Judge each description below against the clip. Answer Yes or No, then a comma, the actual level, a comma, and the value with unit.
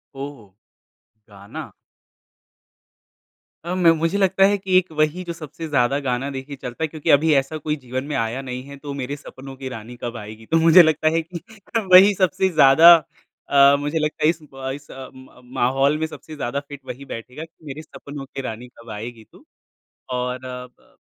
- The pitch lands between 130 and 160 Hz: Yes, medium, 140 Hz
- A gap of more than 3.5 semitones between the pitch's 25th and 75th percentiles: Yes, average, 4.0 semitones